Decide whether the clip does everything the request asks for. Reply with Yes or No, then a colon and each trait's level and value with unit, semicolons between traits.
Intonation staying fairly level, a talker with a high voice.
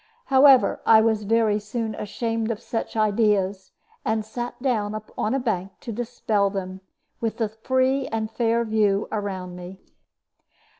Yes: narrow, 2.3 semitones; high, 220 Hz